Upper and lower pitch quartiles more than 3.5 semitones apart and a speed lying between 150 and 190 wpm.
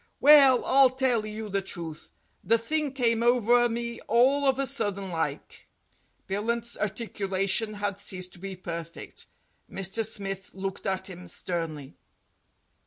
No: average, 4.0 semitones; slow, 135 wpm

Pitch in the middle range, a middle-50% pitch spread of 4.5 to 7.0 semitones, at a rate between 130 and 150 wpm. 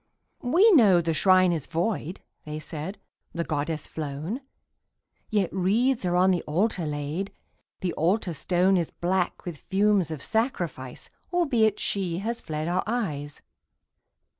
Yes: medium, 180 Hz; average, 4.8 semitones; average, 140 wpm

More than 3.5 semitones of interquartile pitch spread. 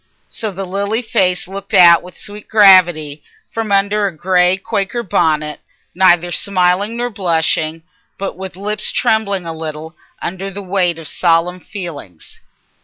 No: average, 3.0 semitones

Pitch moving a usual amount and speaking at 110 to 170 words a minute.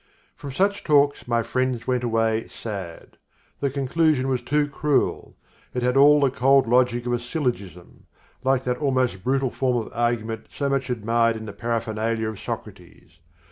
Yes: average, 3.1 semitones; average, 165 wpm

